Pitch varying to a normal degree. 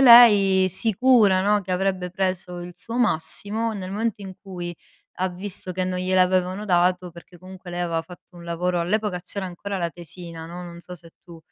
No: narrow, 2.0 semitones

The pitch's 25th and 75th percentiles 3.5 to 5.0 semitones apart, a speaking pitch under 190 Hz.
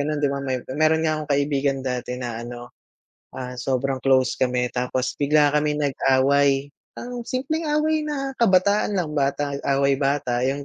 No: average, 2.8 semitones; medium, 140 Hz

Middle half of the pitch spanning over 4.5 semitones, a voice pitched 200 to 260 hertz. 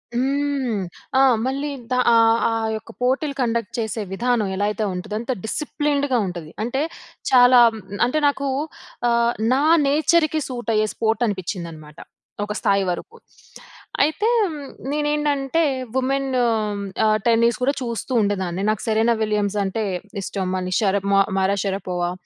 Yes: average, 5.1 semitones; high, 230 Hz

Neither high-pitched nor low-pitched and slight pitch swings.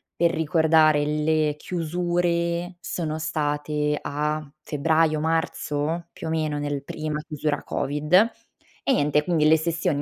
Yes: medium, 155 Hz; narrow, 1.7 semitones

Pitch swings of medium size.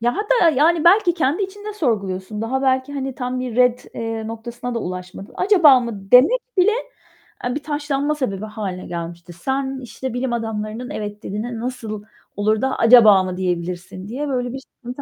Yes: average, 4.7 semitones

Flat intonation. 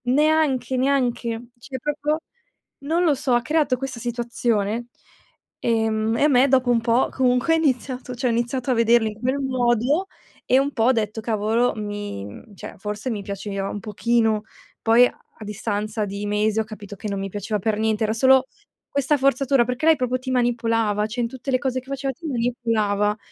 No: average, 3.3 semitones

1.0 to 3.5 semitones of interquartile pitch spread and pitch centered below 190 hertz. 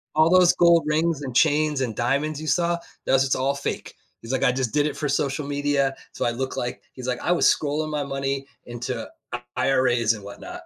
Yes: average, 3.0 semitones; medium, 140 Hz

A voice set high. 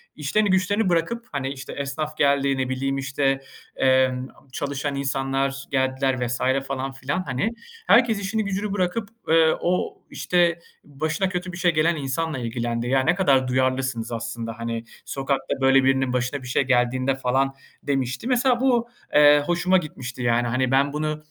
No: low, 135 Hz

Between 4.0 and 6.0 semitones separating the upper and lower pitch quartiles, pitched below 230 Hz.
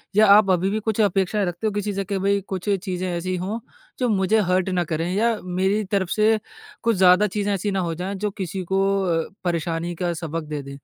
No: average, 2.8 semitones; high, 190 Hz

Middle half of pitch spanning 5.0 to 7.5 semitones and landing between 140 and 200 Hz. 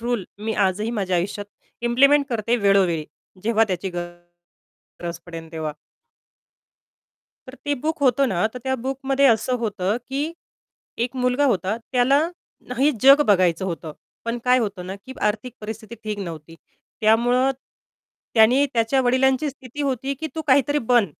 No: wide, 5.5 semitones; high, 230 Hz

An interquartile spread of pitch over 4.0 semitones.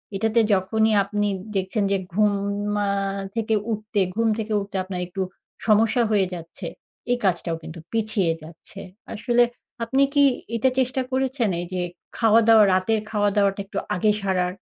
No: average, 3.0 semitones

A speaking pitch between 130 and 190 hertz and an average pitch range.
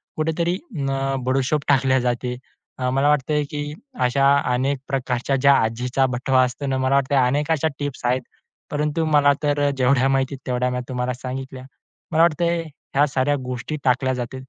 No: low, 135 Hz; narrow, 2.3 semitones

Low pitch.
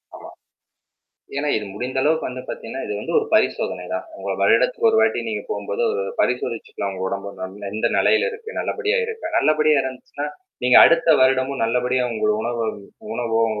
Yes: low, 130 Hz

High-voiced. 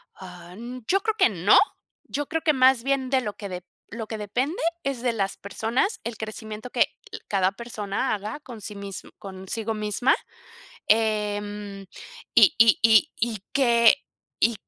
Yes: high, 220 Hz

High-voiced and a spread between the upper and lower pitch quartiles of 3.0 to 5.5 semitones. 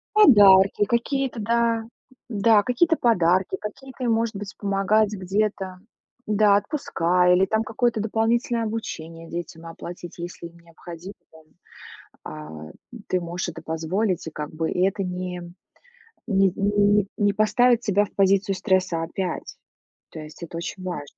Yes: high, 195 Hz; average, 3.9 semitones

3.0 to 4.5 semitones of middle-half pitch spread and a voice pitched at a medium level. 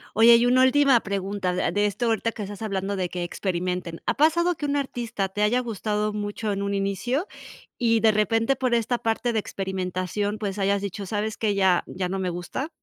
No: average, 3.3 semitones; high, 210 Hz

